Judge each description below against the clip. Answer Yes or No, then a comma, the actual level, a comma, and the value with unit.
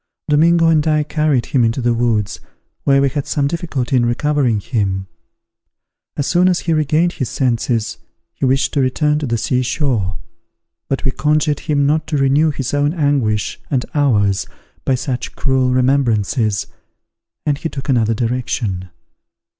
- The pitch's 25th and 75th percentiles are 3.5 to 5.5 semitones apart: Yes, average, 4.0 semitones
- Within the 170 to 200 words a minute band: No, average, 160 wpm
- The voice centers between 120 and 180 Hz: Yes, low, 135 Hz